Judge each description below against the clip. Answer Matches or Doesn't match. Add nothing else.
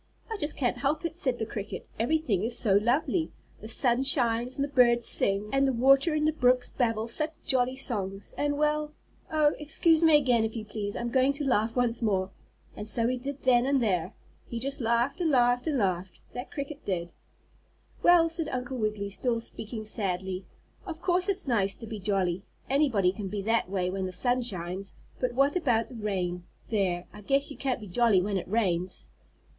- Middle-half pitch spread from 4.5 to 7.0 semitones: Matches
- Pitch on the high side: Matches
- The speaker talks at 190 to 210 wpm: Matches